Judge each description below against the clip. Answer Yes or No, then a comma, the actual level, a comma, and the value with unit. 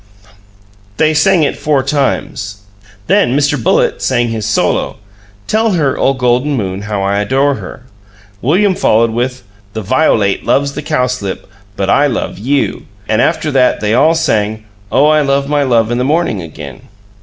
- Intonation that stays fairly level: No, average, 5.2 semitones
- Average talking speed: Yes, average, 165 wpm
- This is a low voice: Yes, low, 130 Hz